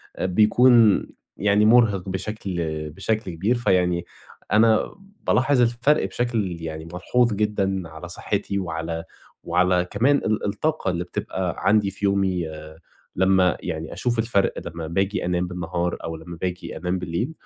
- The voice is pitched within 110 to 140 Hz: No, very low, 95 Hz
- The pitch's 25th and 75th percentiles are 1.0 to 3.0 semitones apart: No, average, 3.6 semitones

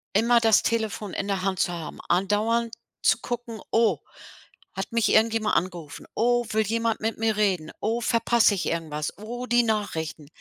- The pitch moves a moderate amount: Yes, average, 3.3 semitones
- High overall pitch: Yes, high, 220 Hz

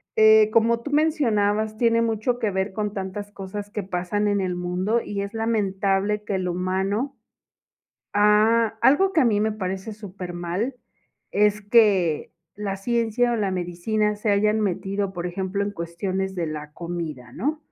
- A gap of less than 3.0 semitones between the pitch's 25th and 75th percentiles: Yes, narrow, 2.6 semitones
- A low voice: No, high, 205 Hz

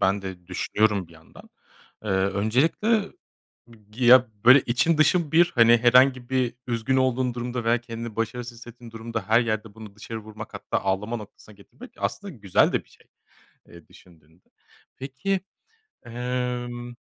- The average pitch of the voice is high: No, low, 120 Hz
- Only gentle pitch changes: No, average, 3.1 semitones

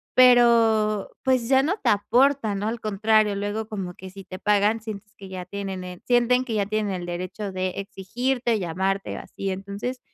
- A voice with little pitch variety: No, average, 3.3 semitones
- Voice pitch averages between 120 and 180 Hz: No, high, 210 Hz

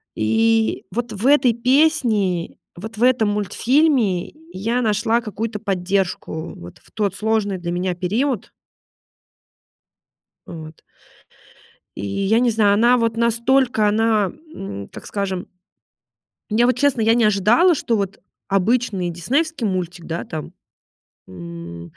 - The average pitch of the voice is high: Yes, high, 215 Hz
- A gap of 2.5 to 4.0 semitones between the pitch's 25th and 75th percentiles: No, average, 4.5 semitones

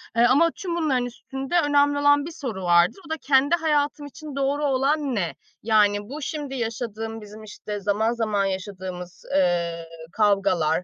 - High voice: Yes, high, 235 Hz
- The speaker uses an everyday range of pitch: No, wide, 6.2 semitones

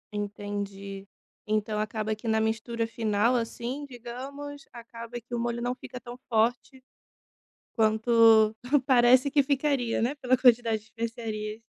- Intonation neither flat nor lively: No, narrow, 2.3 semitones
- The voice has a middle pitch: No, high, 230 Hz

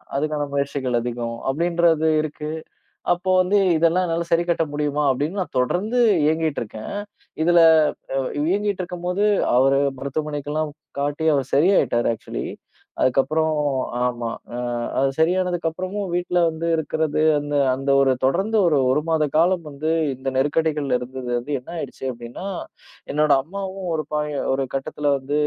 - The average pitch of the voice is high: No, medium, 150 Hz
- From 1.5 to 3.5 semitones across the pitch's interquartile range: No, average, 4.0 semitones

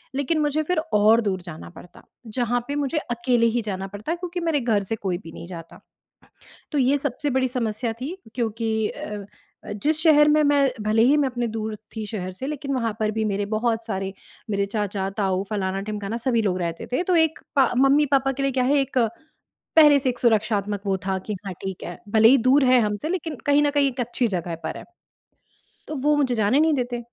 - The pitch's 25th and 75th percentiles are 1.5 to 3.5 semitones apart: No, average, 5.3 semitones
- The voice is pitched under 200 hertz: No, high, 235 Hz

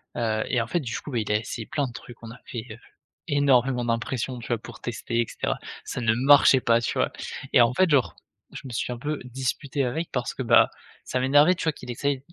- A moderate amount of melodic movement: Yes, average, 3.1 semitones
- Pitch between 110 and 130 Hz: Yes, low, 125 Hz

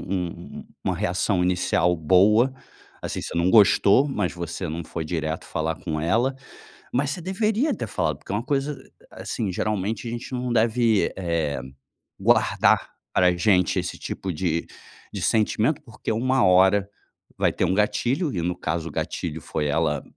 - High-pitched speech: No, very low, 95 Hz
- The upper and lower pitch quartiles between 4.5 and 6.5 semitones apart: Yes, wide, 5.6 semitones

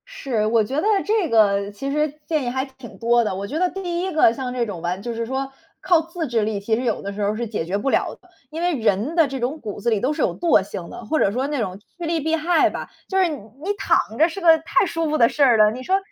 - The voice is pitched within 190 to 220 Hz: No, very high, 265 Hz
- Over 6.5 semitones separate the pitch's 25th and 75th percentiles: Yes, wide, 6.9 semitones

